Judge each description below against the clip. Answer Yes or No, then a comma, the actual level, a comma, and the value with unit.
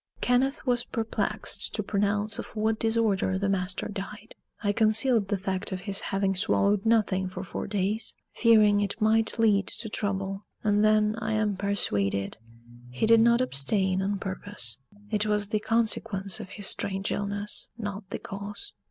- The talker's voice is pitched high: Yes, high, 205 Hz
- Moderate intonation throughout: No, narrow, 2.1 semitones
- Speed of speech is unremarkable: Yes, average, 160 wpm